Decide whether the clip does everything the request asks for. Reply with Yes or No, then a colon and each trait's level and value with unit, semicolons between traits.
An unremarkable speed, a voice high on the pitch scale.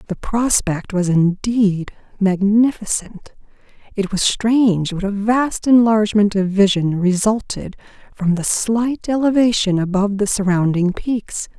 No: slow, 120 wpm; high, 205 Hz